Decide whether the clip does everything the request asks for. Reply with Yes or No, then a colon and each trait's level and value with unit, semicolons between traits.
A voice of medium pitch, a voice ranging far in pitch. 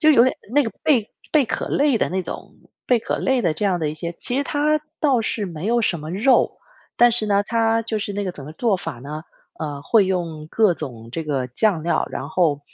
No: high, 200 Hz; wide, 7.1 semitones